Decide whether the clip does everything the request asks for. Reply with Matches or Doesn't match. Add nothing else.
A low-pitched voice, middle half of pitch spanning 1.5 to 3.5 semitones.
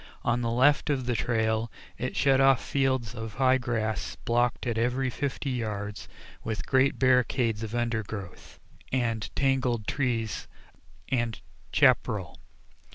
Matches